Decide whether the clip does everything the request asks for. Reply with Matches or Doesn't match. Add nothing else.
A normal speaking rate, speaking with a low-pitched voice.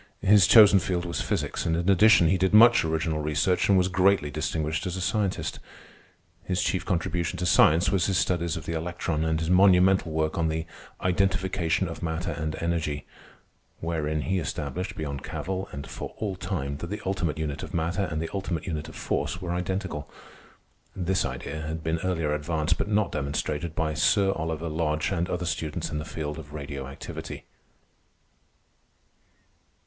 Matches